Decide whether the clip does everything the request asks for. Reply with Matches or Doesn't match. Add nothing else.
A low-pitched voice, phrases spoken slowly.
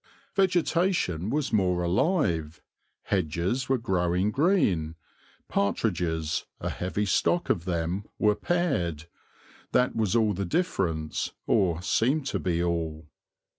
Matches